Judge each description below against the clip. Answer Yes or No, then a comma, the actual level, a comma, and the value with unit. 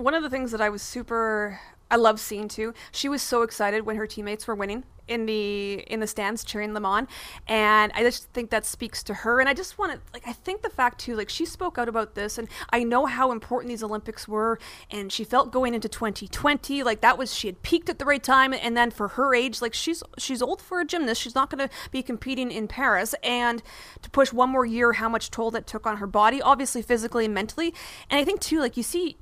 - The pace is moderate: No, fast, 255 wpm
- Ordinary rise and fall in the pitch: Yes, average, 3.3 semitones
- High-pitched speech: Yes, high, 235 Hz